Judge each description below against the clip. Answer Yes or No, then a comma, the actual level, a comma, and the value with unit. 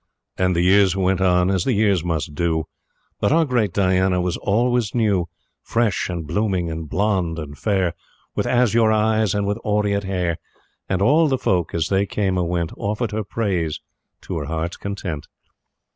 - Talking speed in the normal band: Yes, average, 175 wpm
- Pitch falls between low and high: No, very low, 95 Hz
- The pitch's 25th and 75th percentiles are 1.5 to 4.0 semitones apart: Yes, average, 3.4 semitones